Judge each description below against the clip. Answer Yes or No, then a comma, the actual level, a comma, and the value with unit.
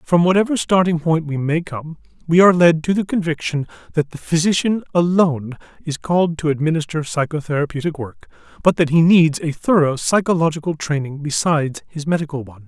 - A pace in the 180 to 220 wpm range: No, average, 165 wpm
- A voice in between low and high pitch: Yes, medium, 160 Hz